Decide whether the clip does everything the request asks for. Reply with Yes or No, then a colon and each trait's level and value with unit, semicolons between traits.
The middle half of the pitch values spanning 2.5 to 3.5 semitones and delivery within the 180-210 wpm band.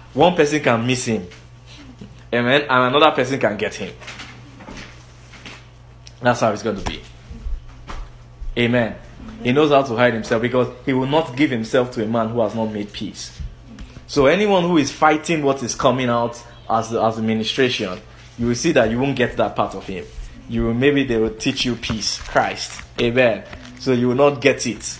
Yes: average, 2.8 semitones; average, 185 wpm